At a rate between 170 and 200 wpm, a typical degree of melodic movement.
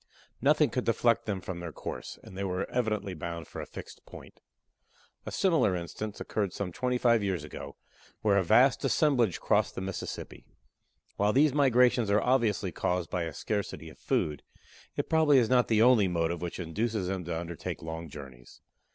No: average, 180 wpm; wide, 5.7 semitones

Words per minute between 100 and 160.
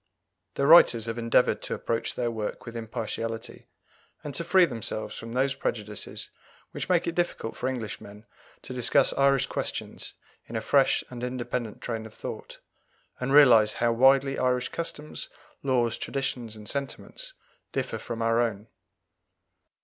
Yes: average, 150 wpm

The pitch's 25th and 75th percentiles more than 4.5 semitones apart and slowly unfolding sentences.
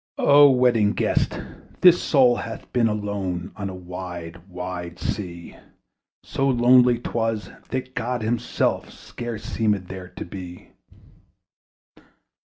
Yes: average, 5.1 semitones; slow, 115 wpm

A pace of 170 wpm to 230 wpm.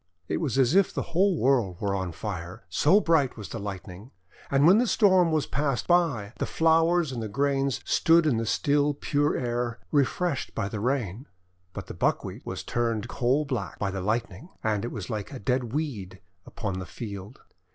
Yes: average, 190 wpm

